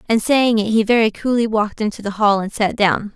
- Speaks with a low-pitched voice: No, high, 215 Hz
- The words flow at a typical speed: No, fast, 245 wpm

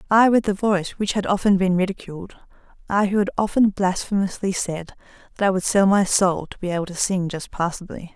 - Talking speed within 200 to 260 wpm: Yes, fast, 205 wpm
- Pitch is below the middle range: No, high, 190 Hz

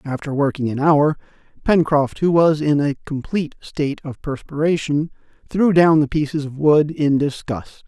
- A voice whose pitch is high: No, medium, 150 Hz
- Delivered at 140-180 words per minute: Yes, average, 160 wpm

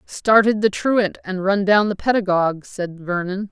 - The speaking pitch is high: Yes, high, 195 Hz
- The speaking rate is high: No, average, 170 wpm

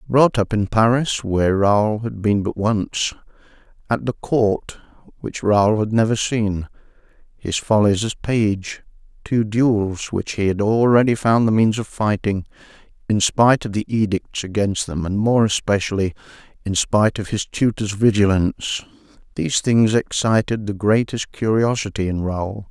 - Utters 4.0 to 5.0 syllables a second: Yes, 4.4 syllables/s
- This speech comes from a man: Yes, male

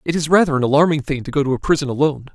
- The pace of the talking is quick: Yes, fast, 305 wpm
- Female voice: No, male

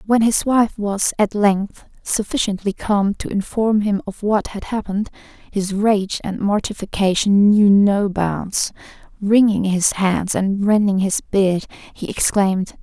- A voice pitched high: Yes, high, 205 Hz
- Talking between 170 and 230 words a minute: No, average, 145 wpm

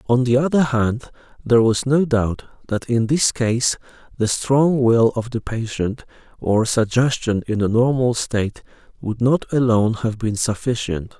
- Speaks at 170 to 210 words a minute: No, average, 160 wpm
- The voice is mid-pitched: No, low, 120 Hz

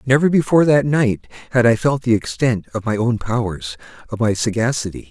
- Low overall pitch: Yes, low, 120 Hz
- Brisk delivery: No, average, 175 wpm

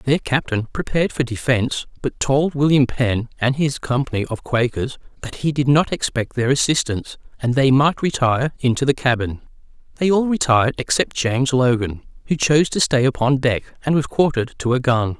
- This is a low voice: Yes, low, 130 Hz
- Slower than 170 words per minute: No, average, 180 wpm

